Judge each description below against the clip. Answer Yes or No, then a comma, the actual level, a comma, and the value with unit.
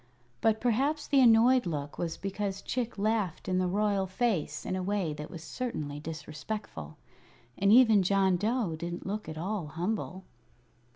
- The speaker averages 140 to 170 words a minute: Yes, average, 160 wpm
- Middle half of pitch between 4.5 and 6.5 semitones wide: Yes, average, 4.8 semitones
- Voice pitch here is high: Yes, high, 195 Hz